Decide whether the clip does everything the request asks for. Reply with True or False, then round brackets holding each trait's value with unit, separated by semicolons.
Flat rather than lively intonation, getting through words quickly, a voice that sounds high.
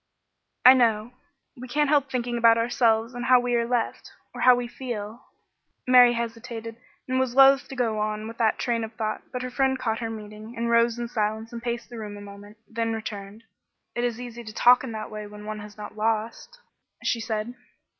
True (2.2 semitones; 215 wpm; 230 Hz)